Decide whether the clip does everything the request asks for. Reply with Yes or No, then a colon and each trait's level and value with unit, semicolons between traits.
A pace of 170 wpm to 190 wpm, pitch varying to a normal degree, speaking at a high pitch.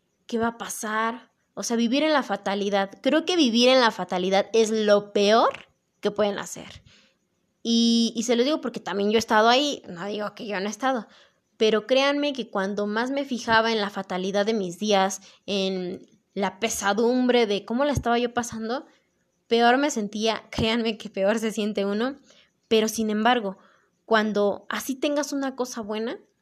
Yes: average, 180 wpm; average, 3.0 semitones; high, 225 Hz